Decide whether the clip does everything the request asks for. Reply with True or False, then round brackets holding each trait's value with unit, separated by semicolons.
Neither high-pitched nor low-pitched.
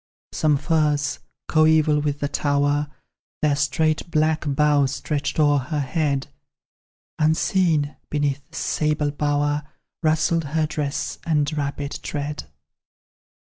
True (150 Hz)